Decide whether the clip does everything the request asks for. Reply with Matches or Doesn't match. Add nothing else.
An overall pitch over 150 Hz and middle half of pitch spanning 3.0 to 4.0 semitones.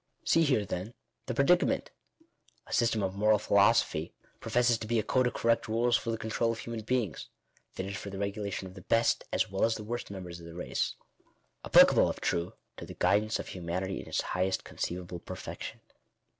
Doesn't match